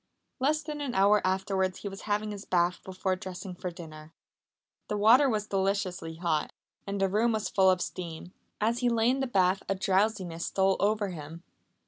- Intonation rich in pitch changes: No, average, 2.8 semitones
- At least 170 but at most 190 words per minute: Yes, average, 185 wpm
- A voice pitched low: No, high, 195 Hz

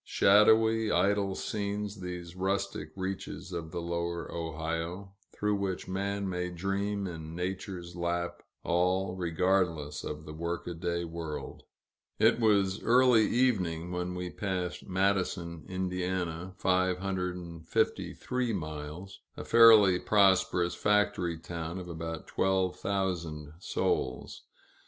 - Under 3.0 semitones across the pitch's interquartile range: Yes, narrow, 2.5 semitones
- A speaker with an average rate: No, slow, 110 wpm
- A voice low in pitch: Yes, very low, 90 Hz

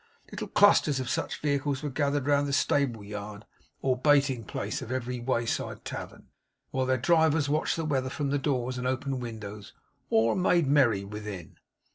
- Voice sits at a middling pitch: No, low, 130 Hz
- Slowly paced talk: No, average, 170 wpm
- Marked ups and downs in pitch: No, average, 3.5 semitones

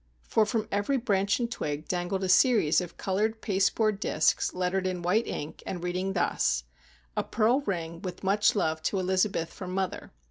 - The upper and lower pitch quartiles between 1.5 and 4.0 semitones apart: Yes, average, 3.1 semitones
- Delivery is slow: No, average, 175 wpm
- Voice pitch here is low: No, high, 190 Hz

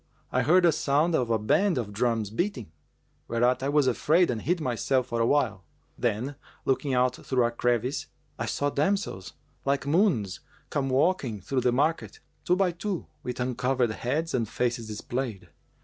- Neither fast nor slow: Yes, average, 170 wpm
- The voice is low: Yes, low, 130 Hz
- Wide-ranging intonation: No, average, 4.2 semitones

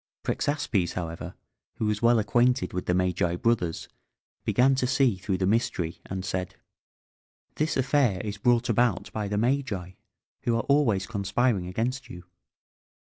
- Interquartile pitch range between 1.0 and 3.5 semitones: No, average, 5.0 semitones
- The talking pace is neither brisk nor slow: Yes, average, 145 wpm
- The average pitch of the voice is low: Yes, low, 105 Hz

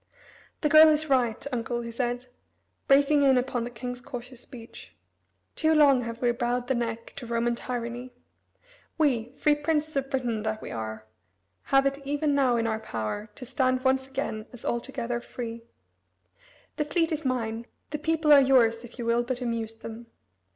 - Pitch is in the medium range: No, high, 245 Hz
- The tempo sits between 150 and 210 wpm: Yes, average, 175 wpm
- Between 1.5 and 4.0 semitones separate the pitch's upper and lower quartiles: Yes, average, 2.9 semitones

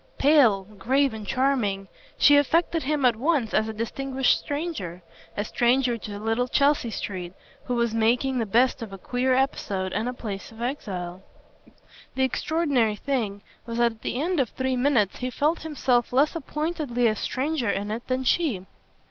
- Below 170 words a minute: No, average, 175 wpm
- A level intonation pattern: No, average, 4.3 semitones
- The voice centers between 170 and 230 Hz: No, high, 245 Hz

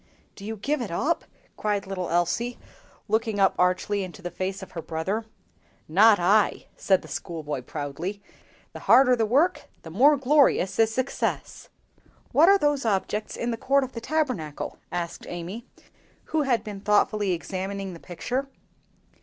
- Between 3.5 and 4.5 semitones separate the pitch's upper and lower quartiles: No, wide, 5.4 semitones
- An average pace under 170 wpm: Yes, average, 160 wpm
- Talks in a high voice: Yes, high, 205 Hz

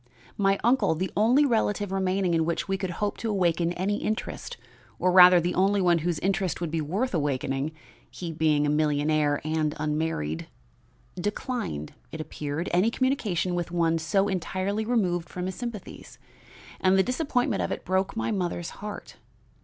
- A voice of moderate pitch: Yes, medium, 180 Hz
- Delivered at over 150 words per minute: Yes, average, 165 wpm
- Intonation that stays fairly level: No, average, 4.1 semitones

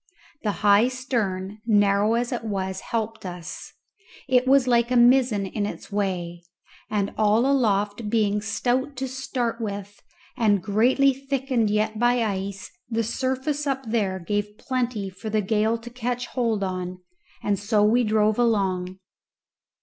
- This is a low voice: No, high, 220 Hz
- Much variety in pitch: No, average, 3.4 semitones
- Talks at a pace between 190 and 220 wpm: No, average, 150 wpm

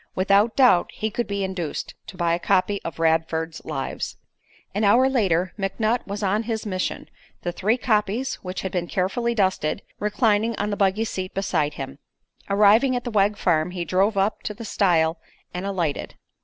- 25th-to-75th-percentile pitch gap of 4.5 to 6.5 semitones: No, average, 3.4 semitones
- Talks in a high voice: Yes, high, 195 Hz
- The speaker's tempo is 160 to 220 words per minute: Yes, average, 180 wpm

